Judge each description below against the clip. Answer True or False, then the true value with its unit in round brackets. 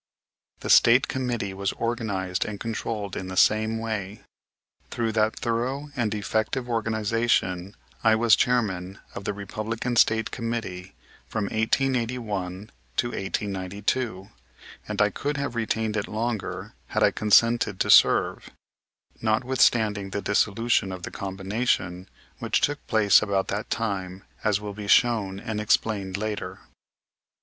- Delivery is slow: True (130 wpm)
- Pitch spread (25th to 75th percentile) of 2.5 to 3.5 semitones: True (2.8 semitones)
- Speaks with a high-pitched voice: False (110 Hz)